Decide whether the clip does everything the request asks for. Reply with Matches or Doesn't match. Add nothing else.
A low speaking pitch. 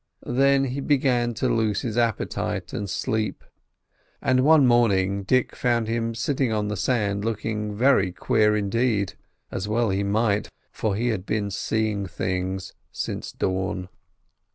Matches